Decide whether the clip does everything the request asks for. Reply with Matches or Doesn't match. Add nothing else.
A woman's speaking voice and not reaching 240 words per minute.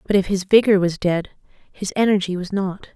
Matches